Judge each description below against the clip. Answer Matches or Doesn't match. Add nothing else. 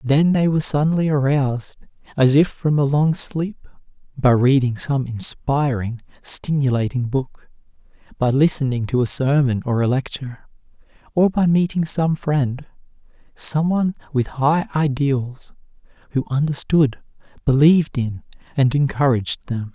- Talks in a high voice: Doesn't match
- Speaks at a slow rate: Matches